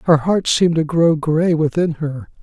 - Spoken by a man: Yes, male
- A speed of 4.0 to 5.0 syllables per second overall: Yes, 4.4 syllables/s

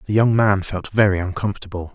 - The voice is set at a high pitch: No, low, 100 Hz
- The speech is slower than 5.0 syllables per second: No, 6.2 syllables/s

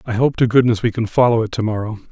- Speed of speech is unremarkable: No, fast, 285 wpm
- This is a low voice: Yes, low, 115 Hz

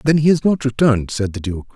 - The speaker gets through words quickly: Yes, fast, 275 wpm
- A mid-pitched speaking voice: No, low, 130 Hz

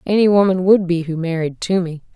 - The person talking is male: No, female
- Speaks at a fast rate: No, average, 195 wpm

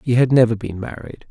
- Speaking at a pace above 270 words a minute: No, fast, 230 wpm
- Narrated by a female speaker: No, male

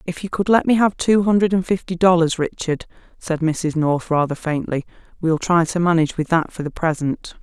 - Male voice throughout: No, female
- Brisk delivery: Yes, fast, 210 wpm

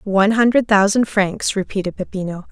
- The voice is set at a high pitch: Yes, high, 205 Hz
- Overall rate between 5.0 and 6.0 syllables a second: Yes, 5.4 syllables/s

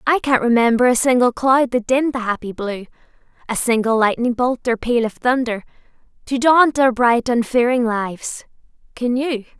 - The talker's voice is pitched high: Yes, high, 245 Hz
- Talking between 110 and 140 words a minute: No, average, 170 wpm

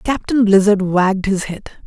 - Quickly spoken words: No, average, 160 wpm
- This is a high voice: Yes, high, 200 Hz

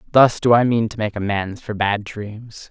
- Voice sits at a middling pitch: No, low, 110 Hz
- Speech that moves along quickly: Yes, fast, 220 wpm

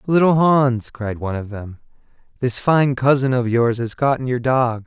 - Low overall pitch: Yes, low, 125 Hz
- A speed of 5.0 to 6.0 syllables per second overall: No, 4.8 syllables/s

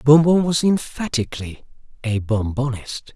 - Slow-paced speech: Yes, slow, 115 wpm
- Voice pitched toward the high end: No, low, 135 Hz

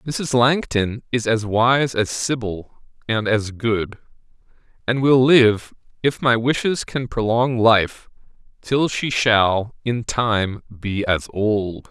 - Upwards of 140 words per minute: No, slow, 135 wpm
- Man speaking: Yes, male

